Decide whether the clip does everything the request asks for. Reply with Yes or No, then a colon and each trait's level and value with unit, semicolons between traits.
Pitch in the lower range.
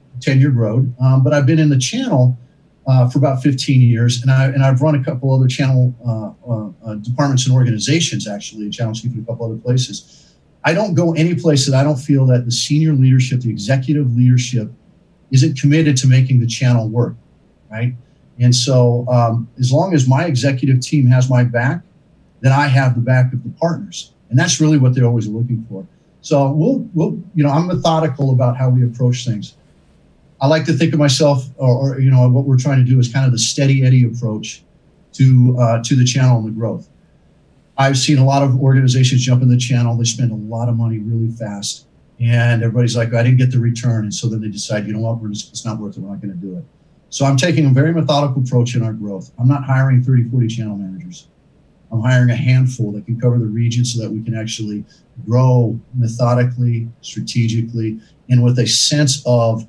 Yes: low, 125 Hz